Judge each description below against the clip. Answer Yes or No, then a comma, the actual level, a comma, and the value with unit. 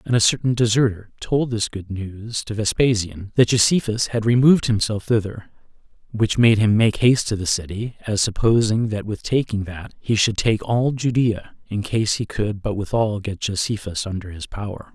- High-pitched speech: No, low, 110 Hz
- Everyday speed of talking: Yes, average, 185 wpm